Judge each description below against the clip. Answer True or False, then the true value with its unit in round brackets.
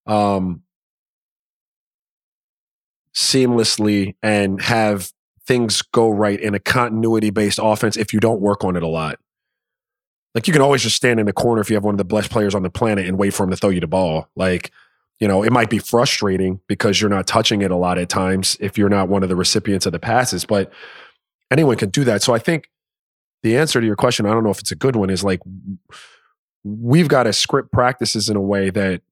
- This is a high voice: False (105 Hz)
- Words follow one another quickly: True (220 wpm)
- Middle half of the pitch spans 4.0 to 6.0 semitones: False (2.8 semitones)